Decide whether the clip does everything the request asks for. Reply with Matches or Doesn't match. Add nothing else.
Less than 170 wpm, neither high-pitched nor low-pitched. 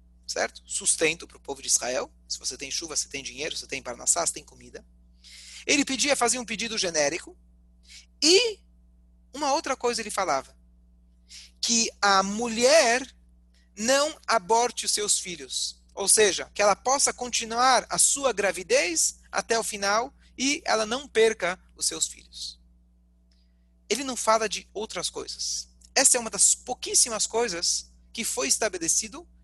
Doesn't match